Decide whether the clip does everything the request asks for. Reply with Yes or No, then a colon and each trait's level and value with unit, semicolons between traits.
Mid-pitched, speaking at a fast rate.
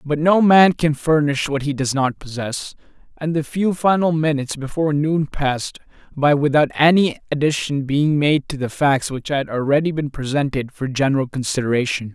No: medium, 145 Hz; average, 175 wpm